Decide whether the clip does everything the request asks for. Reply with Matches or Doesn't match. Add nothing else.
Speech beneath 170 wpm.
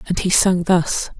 Doesn't match